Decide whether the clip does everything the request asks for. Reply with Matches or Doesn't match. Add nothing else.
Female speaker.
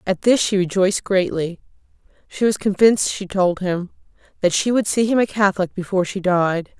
Matches